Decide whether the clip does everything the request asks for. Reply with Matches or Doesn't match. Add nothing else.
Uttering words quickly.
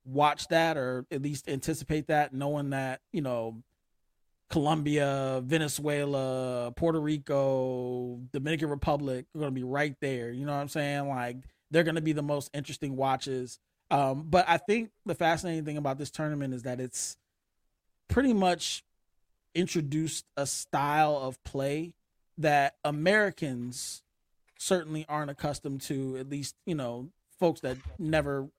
Doesn't match